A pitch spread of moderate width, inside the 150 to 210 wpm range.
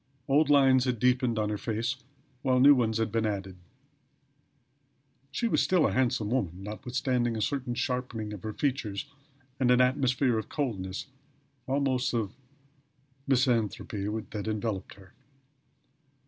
No: average, 3.5 semitones; slow, 135 wpm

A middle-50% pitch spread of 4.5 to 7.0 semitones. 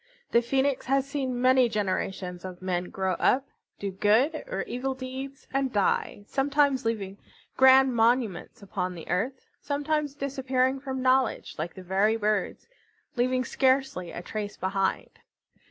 Yes: average, 5.2 semitones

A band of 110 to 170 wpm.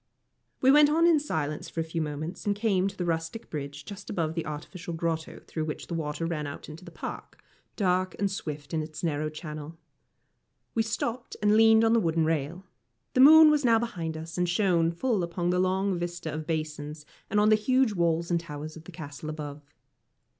No: fast, 205 wpm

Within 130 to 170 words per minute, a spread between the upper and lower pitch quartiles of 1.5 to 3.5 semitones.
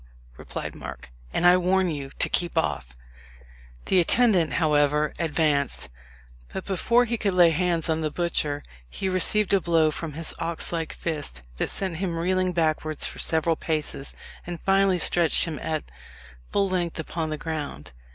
Yes: average, 160 wpm; average, 3.0 semitones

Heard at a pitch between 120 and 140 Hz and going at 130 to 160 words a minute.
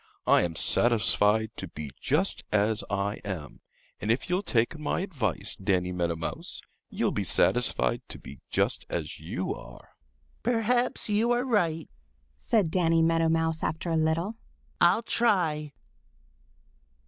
No: medium, 160 Hz; average, 140 wpm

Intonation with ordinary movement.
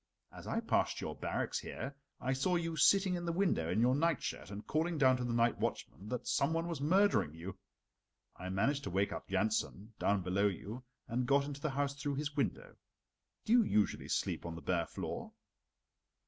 No: wide, 7.8 semitones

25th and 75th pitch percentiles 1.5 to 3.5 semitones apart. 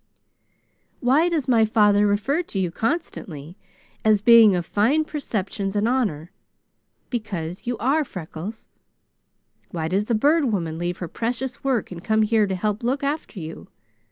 No: average, 5.2 semitones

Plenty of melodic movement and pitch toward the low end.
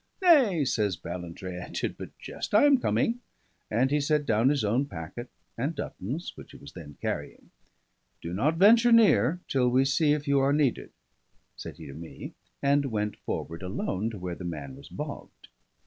Yes: wide, 8.6 semitones; low, 125 Hz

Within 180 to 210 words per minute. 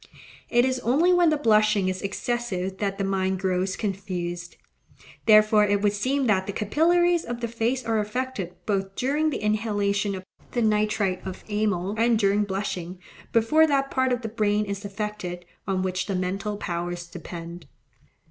No: average, 165 wpm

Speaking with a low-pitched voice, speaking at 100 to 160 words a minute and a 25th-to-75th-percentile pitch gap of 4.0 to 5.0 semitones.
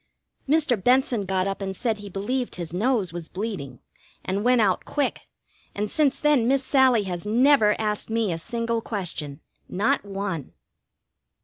No: high, 210 Hz; average, 155 wpm; average, 4.7 semitones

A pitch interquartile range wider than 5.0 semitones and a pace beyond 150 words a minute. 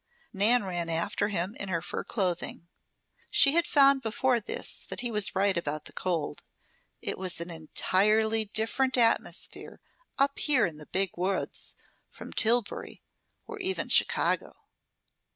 No: wide, 5.4 semitones; average, 145 wpm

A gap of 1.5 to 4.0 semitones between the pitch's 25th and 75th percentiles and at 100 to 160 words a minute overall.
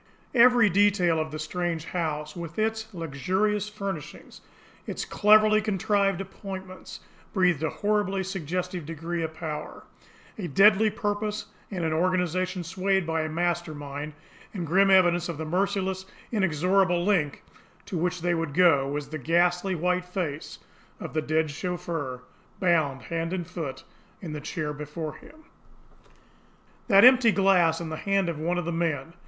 Yes: average, 3.6 semitones; average, 150 wpm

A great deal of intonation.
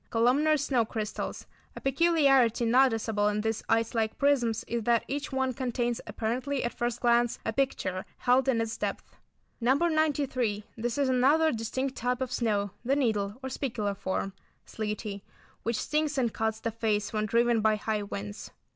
No: average, 3.3 semitones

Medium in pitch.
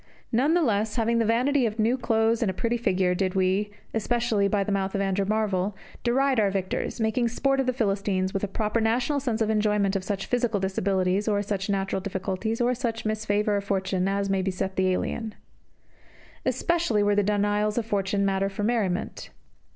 No: high, 210 Hz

